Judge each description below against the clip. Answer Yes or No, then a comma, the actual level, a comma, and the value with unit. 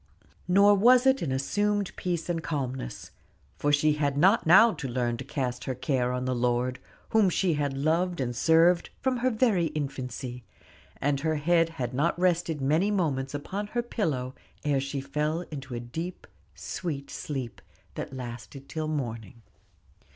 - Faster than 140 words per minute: Yes, average, 165 wpm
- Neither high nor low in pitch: Yes, medium, 150 Hz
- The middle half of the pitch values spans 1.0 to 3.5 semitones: No, average, 5.2 semitones